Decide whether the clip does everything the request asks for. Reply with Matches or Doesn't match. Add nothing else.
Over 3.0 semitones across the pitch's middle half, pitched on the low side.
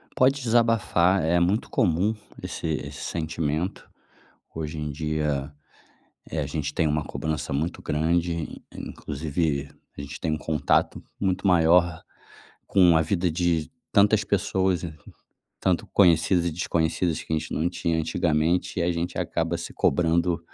Doesn't match